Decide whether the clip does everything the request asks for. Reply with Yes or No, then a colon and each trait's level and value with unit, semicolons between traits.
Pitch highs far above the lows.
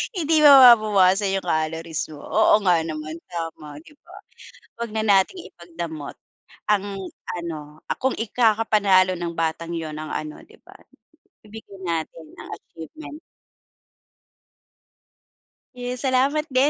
Yes: wide, 6.2 semitones